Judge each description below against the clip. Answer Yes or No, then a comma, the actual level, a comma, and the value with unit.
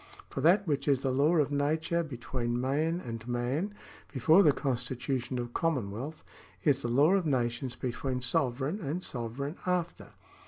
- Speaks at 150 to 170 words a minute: Yes, average, 155 wpm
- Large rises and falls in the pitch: No, average, 4.4 semitones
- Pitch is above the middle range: No, low, 135 Hz